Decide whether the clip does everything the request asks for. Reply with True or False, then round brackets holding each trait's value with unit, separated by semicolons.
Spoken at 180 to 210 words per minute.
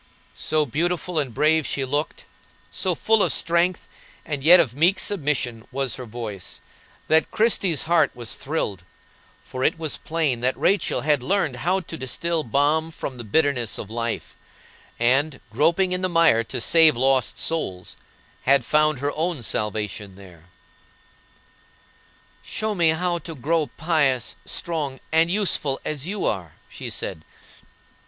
False (145 wpm)